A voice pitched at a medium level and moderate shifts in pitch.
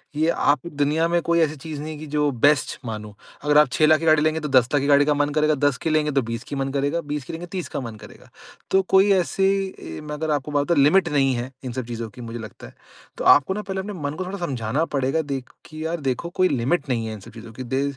Yes: medium, 145 Hz; average, 3.7 semitones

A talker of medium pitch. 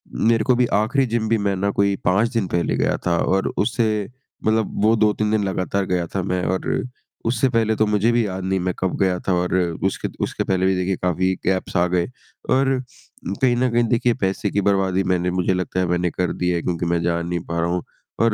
No: very low, 95 Hz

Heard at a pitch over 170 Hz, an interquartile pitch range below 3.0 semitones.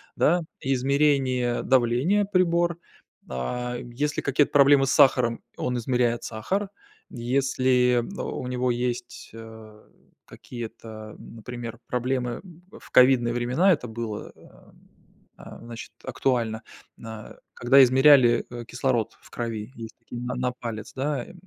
No: low, 125 Hz; narrow, 2.4 semitones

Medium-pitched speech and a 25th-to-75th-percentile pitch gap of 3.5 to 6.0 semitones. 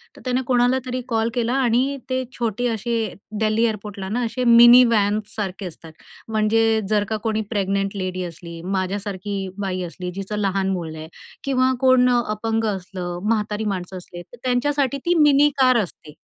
No: high, 215 Hz; average, 4.2 semitones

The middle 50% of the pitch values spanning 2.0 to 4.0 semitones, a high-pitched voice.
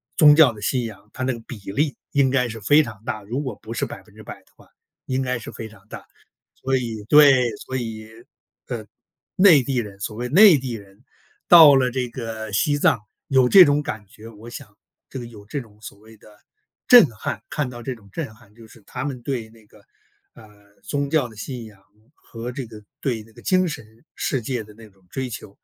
No: average, 3.7 semitones; low, 120 Hz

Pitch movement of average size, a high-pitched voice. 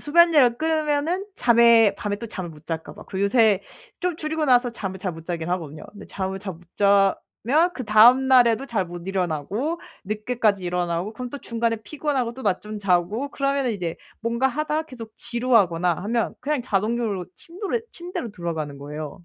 No: wide, 6.0 semitones; high, 225 Hz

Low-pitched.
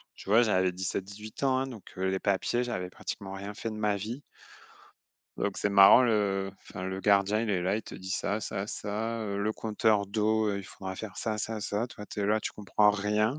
Yes: low, 105 Hz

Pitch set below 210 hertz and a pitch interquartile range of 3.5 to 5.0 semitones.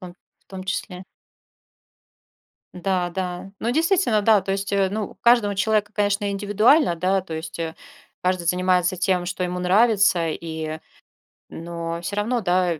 No: medium, 185 Hz; average, 2.7 semitones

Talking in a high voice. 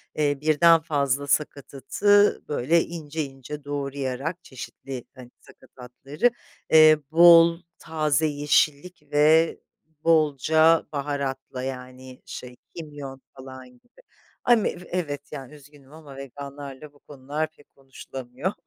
No: medium, 145 Hz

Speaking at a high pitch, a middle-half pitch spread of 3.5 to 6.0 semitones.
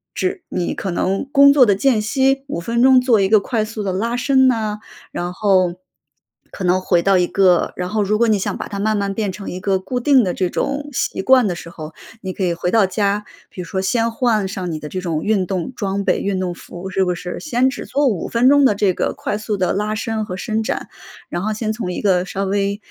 Yes: high, 200 Hz; average, 3.8 semitones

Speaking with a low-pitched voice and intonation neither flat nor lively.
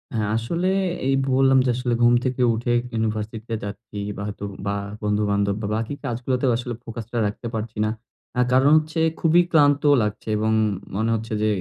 Yes: low, 115 Hz; average, 3.4 semitones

